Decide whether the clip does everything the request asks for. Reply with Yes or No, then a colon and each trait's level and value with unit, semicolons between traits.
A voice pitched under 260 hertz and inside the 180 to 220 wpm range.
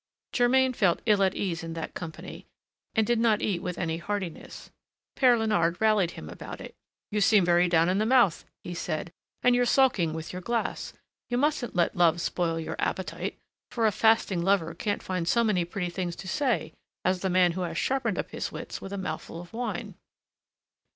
Yes: high, 190 Hz; average, 200 wpm